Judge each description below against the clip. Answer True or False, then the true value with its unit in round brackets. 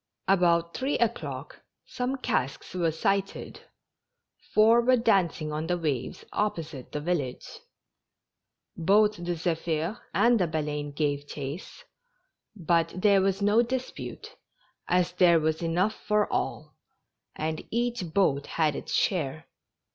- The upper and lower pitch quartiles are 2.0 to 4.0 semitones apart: False (5.0 semitones)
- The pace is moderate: False (125 wpm)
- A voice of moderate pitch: True (175 Hz)